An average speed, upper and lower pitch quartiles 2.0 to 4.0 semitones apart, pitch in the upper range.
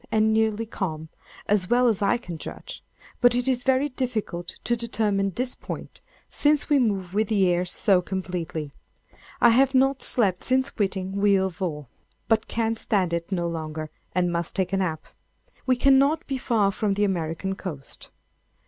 No: average, 165 wpm; average, 5.1 semitones; high, 200 Hz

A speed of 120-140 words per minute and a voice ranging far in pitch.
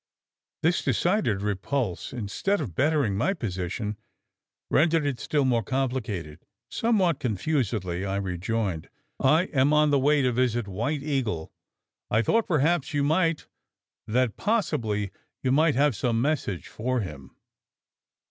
Yes: slow, 135 wpm; wide, 6.6 semitones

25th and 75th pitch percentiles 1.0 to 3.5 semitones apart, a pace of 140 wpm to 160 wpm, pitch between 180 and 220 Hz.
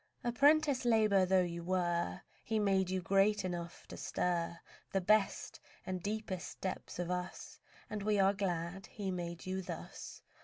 Yes: average, 2.9 semitones; average, 155 wpm; high, 190 Hz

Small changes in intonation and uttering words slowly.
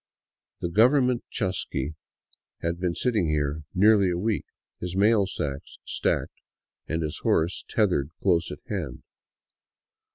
No: average, 4.9 semitones; slow, 125 wpm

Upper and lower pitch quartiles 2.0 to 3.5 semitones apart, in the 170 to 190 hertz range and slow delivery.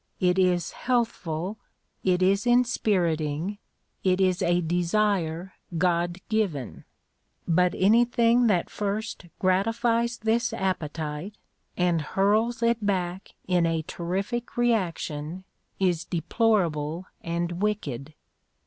No: average, 4.2 semitones; medium, 185 Hz; slow, 100 wpm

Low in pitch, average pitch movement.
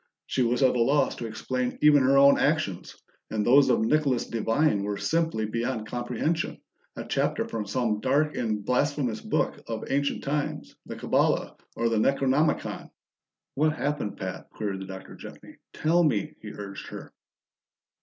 Yes: low, 125 Hz; average, 4.8 semitones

